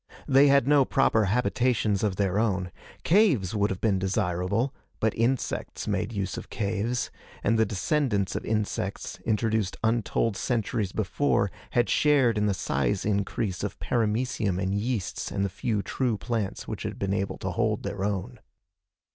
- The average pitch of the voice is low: Yes, low, 105 Hz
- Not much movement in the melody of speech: No, average, 3.5 semitones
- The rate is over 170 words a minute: No, average, 160 wpm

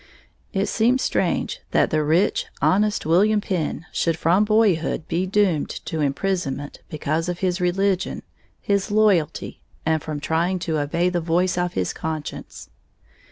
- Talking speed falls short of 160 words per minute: Yes, average, 145 wpm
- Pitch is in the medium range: Yes, medium, 175 Hz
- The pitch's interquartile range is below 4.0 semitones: Yes, average, 3.6 semitones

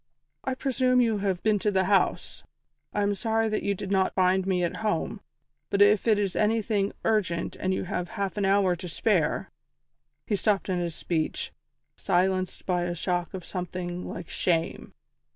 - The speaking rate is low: No, average, 185 wpm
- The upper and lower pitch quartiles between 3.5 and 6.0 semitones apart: No, average, 2.7 semitones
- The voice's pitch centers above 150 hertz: Yes, high, 190 Hz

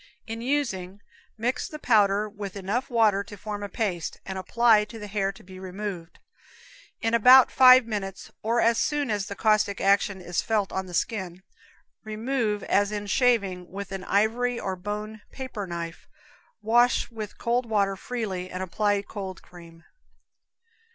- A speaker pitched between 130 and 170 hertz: No, high, 210 Hz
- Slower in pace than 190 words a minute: Yes, average, 160 wpm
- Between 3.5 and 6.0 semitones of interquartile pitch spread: No, average, 3.1 semitones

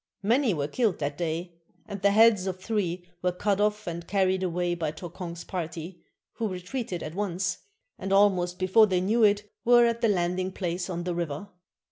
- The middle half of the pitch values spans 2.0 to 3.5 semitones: Yes, average, 3.1 semitones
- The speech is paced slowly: No, average, 185 wpm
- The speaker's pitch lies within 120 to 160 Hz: No, medium, 185 Hz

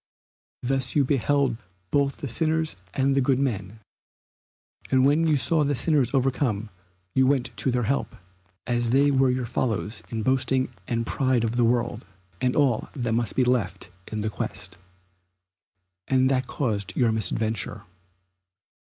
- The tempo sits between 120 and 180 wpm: Yes, average, 155 wpm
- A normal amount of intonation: Yes, average, 3.1 semitones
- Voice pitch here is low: Yes, low, 125 Hz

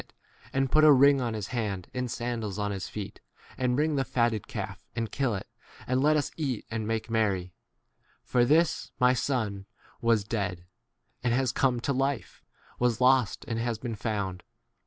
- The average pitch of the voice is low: Yes, low, 120 Hz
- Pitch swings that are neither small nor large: Yes, average, 3.5 semitones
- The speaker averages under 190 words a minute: No, average, 195 wpm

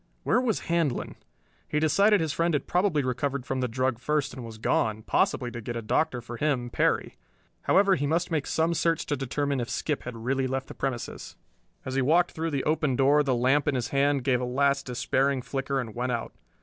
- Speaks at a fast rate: Yes, fast, 215 wpm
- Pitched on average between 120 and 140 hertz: Yes, low, 135 Hz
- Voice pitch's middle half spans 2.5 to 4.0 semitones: Yes, average, 3.4 semitones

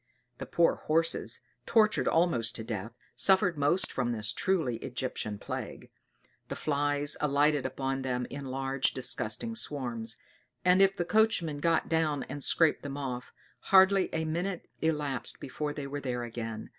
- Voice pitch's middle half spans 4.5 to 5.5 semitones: Yes, average, 4.8 semitones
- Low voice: No, medium, 145 Hz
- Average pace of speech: Yes, average, 150 wpm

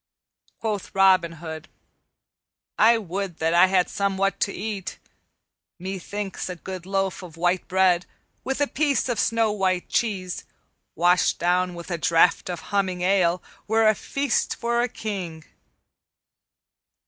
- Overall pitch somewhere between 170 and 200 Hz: Yes, high, 190 Hz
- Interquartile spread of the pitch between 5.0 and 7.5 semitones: No, average, 2.8 semitones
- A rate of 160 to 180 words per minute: No, slow, 135 wpm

